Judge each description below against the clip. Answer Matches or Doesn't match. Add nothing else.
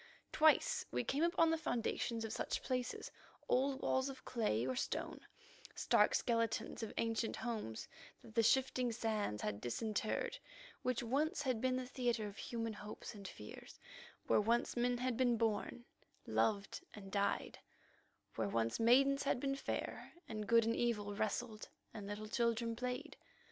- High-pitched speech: Matches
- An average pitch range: Matches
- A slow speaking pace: Doesn't match